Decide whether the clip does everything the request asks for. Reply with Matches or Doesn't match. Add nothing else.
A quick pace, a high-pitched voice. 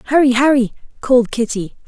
Doesn't match